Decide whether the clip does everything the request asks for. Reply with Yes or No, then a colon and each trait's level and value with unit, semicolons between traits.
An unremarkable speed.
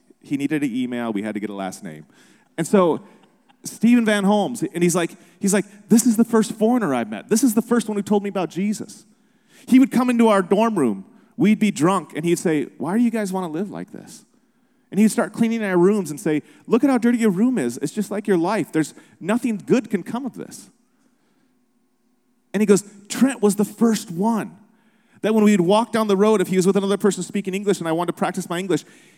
No: fast, 240 wpm